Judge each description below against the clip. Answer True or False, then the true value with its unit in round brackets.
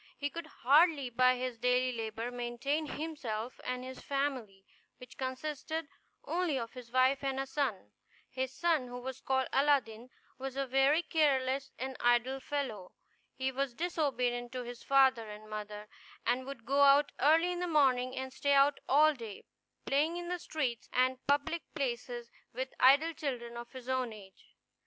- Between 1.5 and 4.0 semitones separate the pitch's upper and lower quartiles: True (2.7 semitones)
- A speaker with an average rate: True (165 wpm)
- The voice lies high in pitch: True (260 Hz)